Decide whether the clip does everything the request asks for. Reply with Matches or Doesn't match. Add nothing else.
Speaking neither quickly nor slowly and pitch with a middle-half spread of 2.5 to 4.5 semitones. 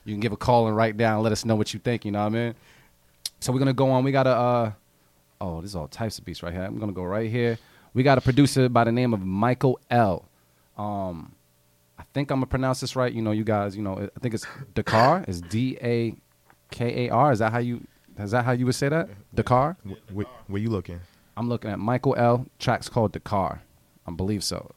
Doesn't match